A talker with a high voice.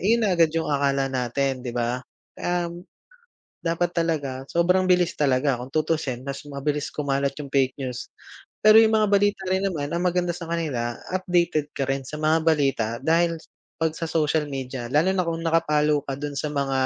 No: medium, 150 Hz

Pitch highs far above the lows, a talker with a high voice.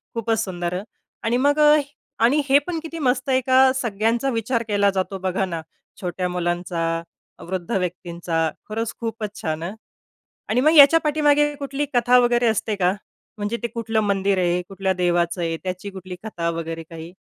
Yes: wide, 5.7 semitones; high, 205 Hz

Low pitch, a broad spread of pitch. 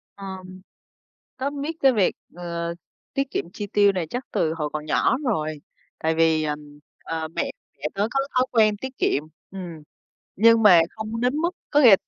No: high, 195 Hz; wide, 7.0 semitones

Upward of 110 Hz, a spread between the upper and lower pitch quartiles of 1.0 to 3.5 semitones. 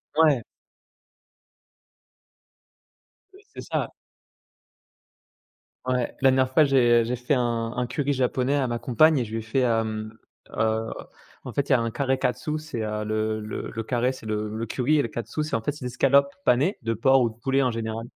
Yes: low, 125 Hz; average, 3.0 semitones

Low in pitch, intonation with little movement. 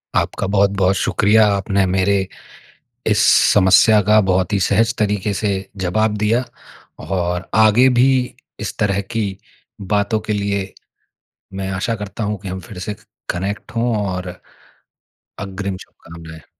Yes: low, 100 Hz; narrow, 2.0 semitones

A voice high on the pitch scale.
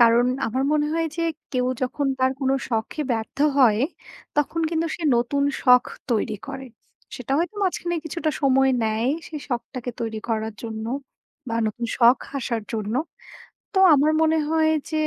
Yes: very high, 260 Hz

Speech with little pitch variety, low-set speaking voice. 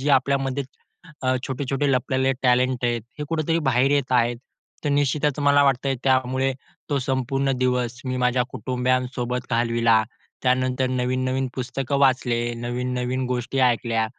Yes: narrow, 1.4 semitones; low, 130 Hz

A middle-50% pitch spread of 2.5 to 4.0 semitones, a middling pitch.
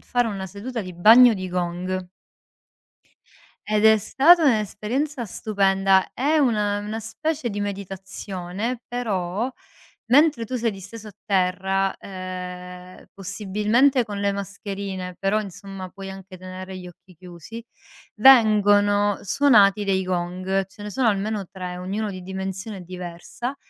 No: average, 2.8 semitones; high, 200 Hz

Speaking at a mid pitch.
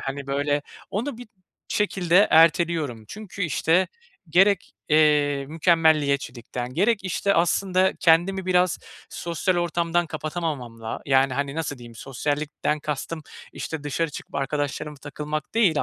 Yes: medium, 155 Hz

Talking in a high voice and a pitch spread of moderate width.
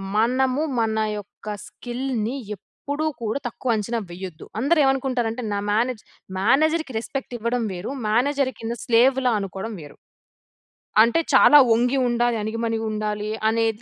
Yes: high, 235 Hz; average, 3.1 semitones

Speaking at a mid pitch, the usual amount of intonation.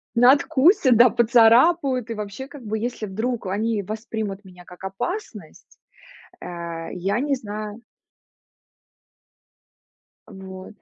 No: high, 220 Hz; average, 4.4 semitones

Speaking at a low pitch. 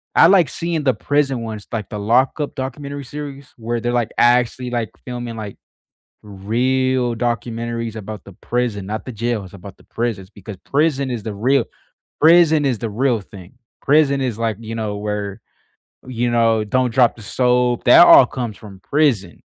Yes: low, 120 Hz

